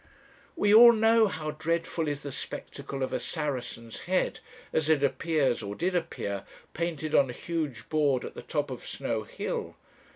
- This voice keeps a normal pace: Yes, average, 170 wpm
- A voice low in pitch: No, medium, 150 Hz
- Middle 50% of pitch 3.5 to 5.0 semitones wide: Yes, average, 3.9 semitones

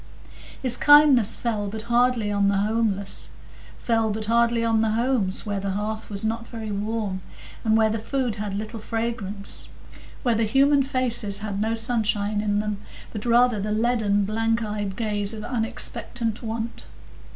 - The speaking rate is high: No, average, 160 wpm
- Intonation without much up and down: Yes, narrow, 2.1 semitones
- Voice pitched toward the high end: Yes, high, 220 Hz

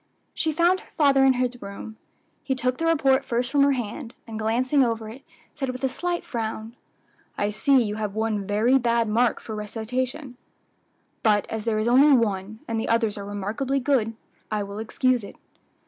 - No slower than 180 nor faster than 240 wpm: Yes, average, 190 wpm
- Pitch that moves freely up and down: No, average, 3.6 semitones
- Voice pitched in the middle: No, high, 235 Hz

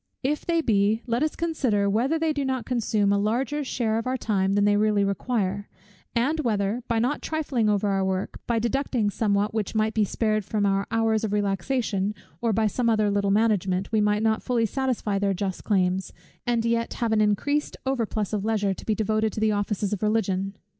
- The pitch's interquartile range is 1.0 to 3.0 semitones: Yes, average, 2.7 semitones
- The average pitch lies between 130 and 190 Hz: No, high, 215 Hz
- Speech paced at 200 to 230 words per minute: Yes, fast, 205 wpm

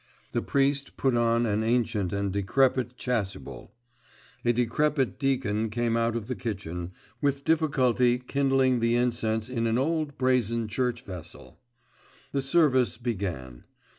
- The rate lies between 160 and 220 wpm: No, slow, 135 wpm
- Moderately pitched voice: No, low, 120 Hz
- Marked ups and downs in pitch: No, average, 3.2 semitones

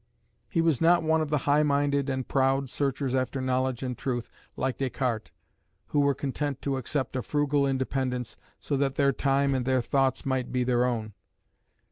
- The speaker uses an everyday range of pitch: No, narrow, 1.7 semitones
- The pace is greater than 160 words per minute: Yes, average, 180 wpm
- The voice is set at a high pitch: No, low, 135 Hz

